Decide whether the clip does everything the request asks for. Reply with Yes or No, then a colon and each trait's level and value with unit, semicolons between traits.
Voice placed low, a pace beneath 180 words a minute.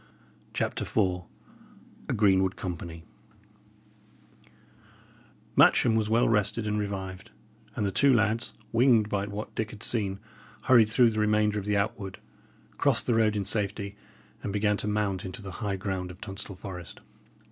Yes: low, 105 Hz; average, 150 wpm